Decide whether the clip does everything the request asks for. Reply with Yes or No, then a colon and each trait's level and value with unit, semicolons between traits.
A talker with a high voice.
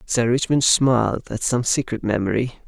No: low, 120 Hz